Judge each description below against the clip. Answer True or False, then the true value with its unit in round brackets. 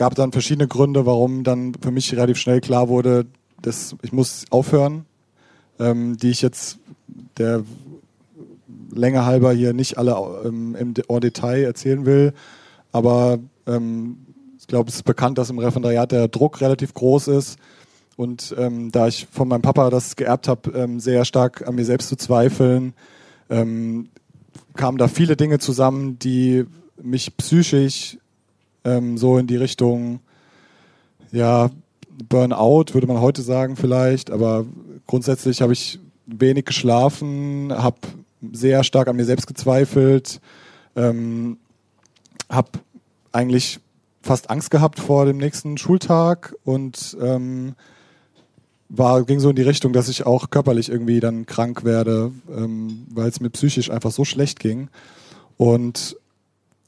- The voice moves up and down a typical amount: False (2.0 semitones)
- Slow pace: False (145 wpm)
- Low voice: True (125 Hz)